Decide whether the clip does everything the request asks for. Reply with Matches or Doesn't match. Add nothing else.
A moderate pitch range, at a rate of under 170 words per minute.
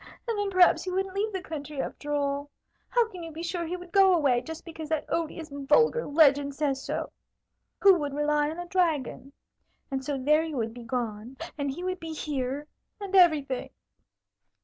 Doesn't match